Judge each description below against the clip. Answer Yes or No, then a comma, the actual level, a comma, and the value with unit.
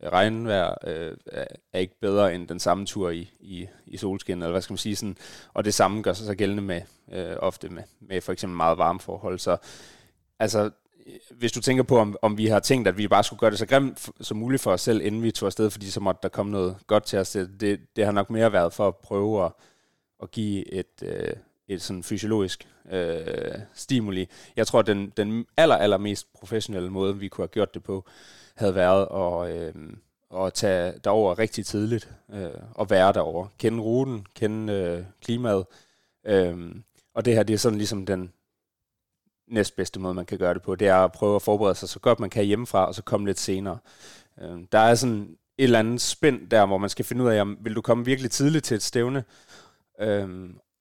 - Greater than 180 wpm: Yes, average, 220 wpm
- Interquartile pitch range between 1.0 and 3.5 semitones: Yes, average, 2.8 semitones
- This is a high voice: No, low, 105 Hz